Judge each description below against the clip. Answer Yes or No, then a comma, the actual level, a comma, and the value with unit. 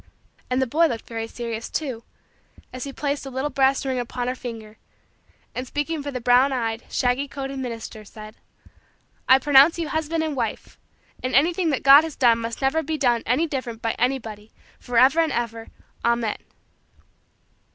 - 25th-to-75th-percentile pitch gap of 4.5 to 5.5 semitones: No, average, 3.5 semitones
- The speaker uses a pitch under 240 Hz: No, very high, 255 Hz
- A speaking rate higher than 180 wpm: No, average, 170 wpm